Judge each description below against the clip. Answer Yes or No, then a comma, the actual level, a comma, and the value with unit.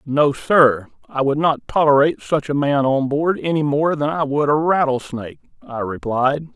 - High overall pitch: No, medium, 145 Hz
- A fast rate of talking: No, average, 185 wpm